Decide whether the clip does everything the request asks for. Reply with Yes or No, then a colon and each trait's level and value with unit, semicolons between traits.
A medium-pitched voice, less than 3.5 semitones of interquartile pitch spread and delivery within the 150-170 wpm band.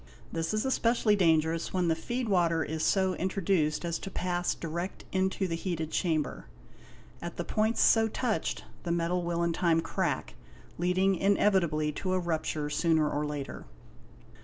Yes: medium, 175 Hz; average, 2.8 semitones; average, 160 wpm